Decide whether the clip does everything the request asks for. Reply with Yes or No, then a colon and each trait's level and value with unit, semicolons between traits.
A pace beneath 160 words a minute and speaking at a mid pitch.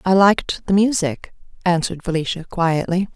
Yes: slow, 135 wpm; medium, 180 Hz